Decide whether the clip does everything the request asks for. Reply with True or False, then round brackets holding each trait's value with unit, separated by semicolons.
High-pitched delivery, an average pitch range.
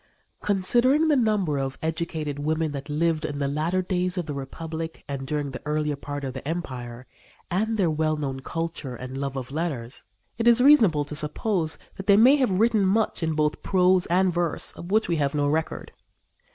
False (160 Hz; 4.6 semitones)